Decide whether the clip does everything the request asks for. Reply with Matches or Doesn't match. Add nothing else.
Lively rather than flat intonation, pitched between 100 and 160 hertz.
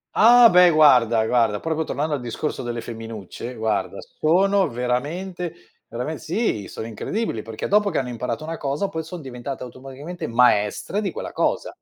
Matches